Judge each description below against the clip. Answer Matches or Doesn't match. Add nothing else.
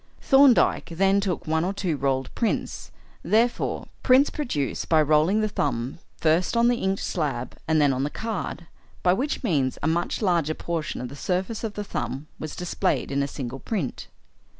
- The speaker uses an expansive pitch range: Matches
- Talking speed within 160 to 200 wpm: Matches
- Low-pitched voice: Doesn't match